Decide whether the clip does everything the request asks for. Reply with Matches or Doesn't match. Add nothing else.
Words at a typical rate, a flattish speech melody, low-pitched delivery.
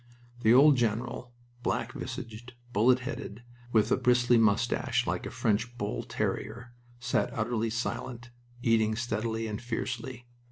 Doesn't match